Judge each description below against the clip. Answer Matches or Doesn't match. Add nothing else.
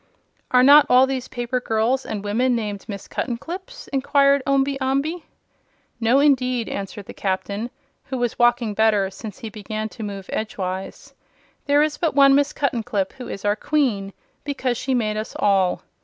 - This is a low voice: Doesn't match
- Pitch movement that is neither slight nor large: Matches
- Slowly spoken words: Doesn't match